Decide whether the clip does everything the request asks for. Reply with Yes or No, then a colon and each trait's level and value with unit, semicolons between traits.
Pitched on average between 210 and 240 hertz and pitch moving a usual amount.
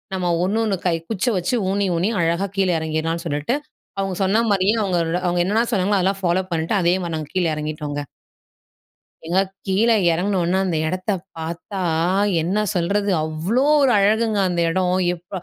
No: medium, 185 Hz; average, 3.1 semitones